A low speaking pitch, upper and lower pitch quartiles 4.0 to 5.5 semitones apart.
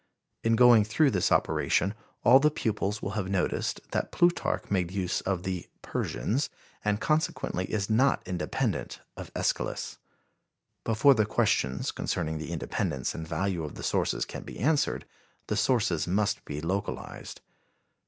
Yes: low, 100 Hz; average, 4.5 semitones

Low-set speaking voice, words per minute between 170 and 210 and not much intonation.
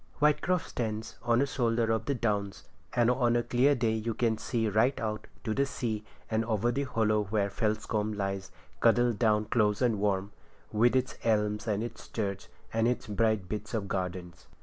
Yes: low, 110 Hz; average, 180 wpm; narrow, 2.3 semitones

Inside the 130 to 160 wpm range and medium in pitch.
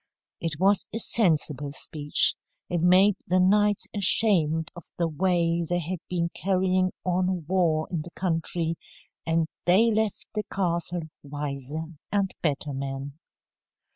Yes: slow, 135 wpm; medium, 170 Hz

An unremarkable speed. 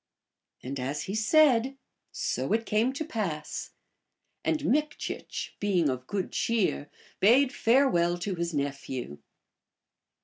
No: slow, 115 wpm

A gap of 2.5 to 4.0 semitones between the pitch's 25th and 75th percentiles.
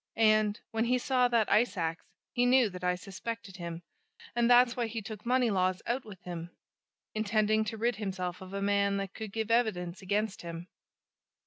Yes: average, 3.7 semitones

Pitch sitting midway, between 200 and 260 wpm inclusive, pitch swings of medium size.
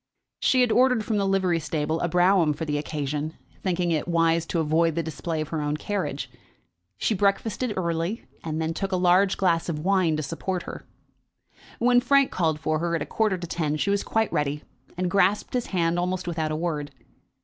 Yes: medium, 170 Hz; fast, 205 wpm; average, 3.8 semitones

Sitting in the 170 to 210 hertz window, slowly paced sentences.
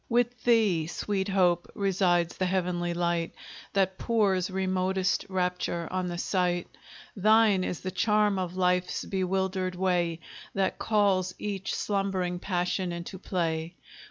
Yes: medium, 185 Hz; slow, 130 wpm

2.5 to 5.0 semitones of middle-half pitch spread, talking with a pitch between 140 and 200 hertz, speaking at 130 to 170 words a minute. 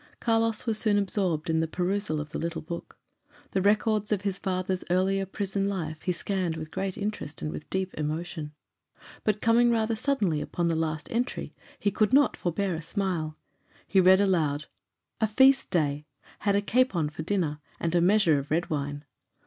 No: average, 4.5 semitones; medium, 185 Hz; average, 180 wpm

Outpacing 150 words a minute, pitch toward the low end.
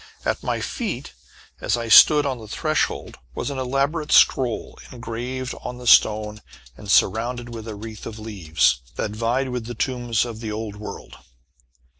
Yes: average, 165 wpm; low, 120 Hz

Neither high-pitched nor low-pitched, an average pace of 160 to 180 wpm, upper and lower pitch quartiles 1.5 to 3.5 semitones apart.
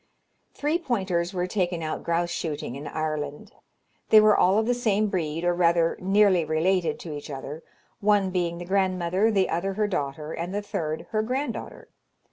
No: medium, 180 Hz; average, 175 wpm; average, 3.9 semitones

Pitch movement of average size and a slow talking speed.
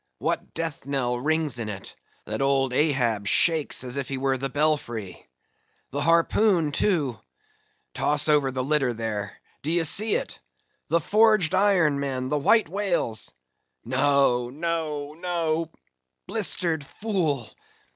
Yes: average, 4.9 semitones; slow, 115 wpm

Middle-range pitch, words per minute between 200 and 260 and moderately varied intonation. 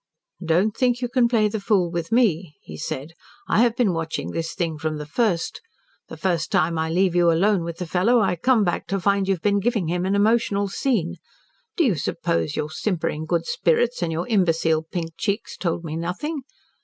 Yes: medium, 180 Hz; fast, 205 wpm; average, 4.4 semitones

